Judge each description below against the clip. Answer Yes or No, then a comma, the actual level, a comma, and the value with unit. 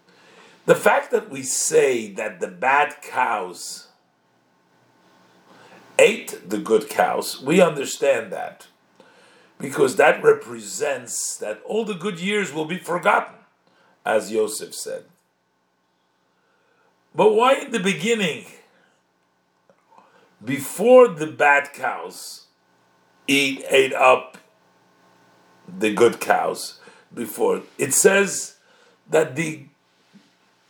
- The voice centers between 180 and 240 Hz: Yes, medium, 185 Hz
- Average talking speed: No, slow, 100 wpm